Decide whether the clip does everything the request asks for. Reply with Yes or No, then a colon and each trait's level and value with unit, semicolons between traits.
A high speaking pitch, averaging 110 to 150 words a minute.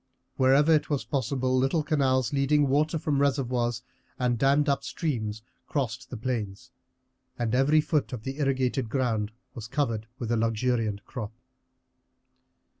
No: low, 130 Hz; average, 140 wpm